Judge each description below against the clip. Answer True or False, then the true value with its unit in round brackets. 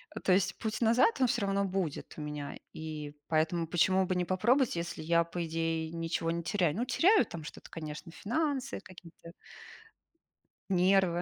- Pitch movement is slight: False (3.4 semitones)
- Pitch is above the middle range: False (175 Hz)